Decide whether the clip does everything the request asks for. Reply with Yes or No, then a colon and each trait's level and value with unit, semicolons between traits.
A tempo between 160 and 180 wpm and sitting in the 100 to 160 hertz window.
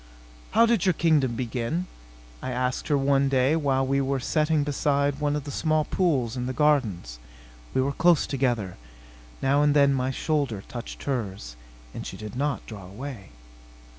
Yes: average, 170 wpm; low, 135 Hz